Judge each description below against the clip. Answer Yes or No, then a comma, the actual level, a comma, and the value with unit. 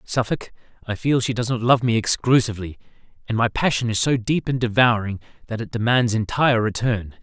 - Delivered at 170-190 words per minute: Yes, average, 185 wpm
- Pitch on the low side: Yes, low, 115 Hz